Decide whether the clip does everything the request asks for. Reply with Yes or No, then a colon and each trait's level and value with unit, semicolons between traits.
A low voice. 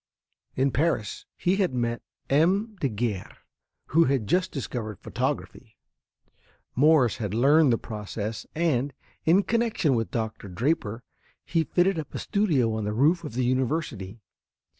Yes: low, 130 Hz